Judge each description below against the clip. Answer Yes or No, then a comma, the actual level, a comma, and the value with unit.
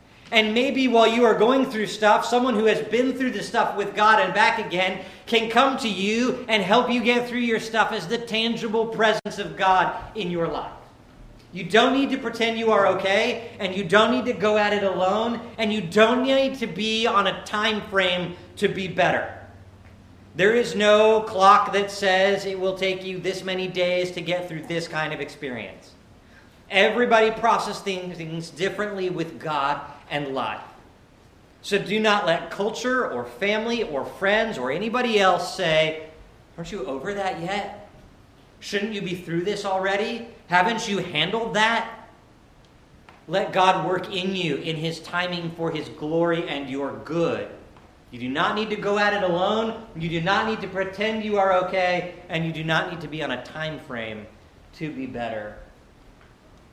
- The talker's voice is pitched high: Yes, high, 195 Hz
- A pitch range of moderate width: Yes, average, 4.7 semitones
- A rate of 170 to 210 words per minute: Yes, average, 180 wpm